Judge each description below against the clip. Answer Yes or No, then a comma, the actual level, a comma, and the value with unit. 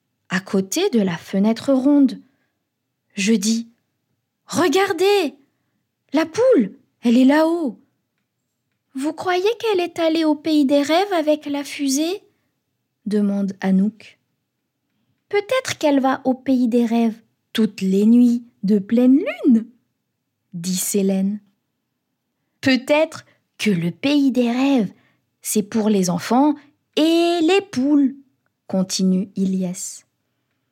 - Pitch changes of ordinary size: No, wide, 6.9 semitones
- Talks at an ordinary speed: No, slow, 115 wpm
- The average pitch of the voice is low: No, very high, 250 Hz